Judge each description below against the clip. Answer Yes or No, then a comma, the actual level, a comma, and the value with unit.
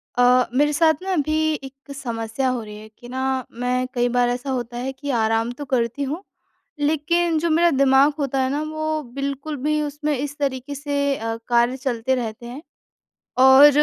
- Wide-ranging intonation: No, average, 3.0 semitones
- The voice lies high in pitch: Yes, very high, 270 Hz